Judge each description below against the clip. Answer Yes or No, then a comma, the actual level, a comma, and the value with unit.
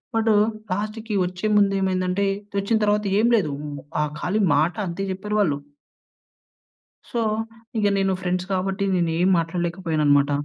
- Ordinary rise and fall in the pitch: Yes, average, 3.5 semitones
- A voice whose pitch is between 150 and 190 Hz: Yes, medium, 185 Hz